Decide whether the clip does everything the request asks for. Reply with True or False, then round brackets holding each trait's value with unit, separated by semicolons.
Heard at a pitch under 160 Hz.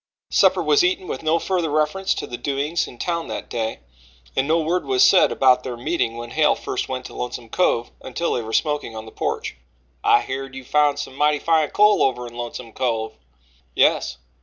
True (135 Hz)